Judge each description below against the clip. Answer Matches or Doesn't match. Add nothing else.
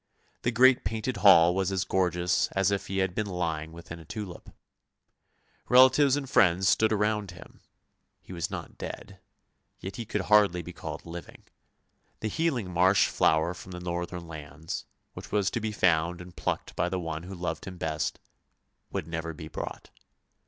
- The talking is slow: Doesn't match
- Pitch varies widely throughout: Doesn't match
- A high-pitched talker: Doesn't match